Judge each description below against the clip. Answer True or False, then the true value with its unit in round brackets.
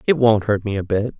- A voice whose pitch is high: False (110 Hz)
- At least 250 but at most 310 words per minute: True (300 wpm)